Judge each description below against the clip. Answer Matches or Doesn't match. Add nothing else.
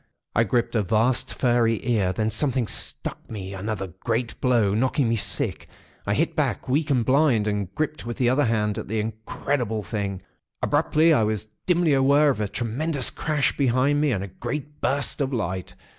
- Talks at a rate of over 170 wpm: Matches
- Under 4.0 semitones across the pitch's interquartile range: Doesn't match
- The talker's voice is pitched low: Matches